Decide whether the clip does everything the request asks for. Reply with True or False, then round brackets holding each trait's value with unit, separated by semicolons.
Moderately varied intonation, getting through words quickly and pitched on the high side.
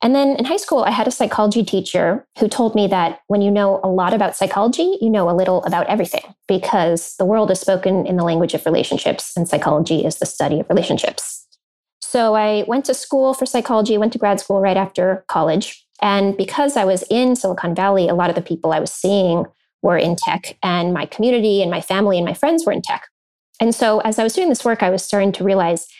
True (3.7 semitones; 235 wpm; 195 Hz)